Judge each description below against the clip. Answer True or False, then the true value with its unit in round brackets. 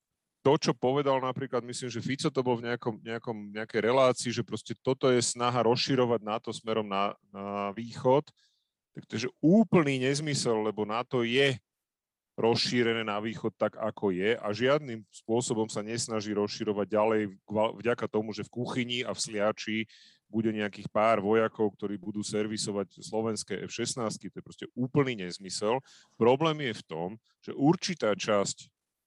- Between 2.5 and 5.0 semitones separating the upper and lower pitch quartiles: True (2.8 semitones)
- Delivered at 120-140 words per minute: False (155 wpm)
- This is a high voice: False (115 Hz)